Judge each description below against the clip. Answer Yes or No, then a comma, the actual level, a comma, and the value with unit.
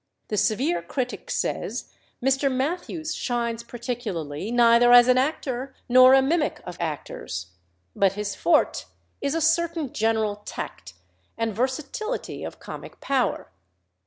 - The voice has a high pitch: Yes, high, 245 Hz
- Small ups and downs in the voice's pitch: No, average, 4.1 semitones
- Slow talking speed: Yes, slow, 130 wpm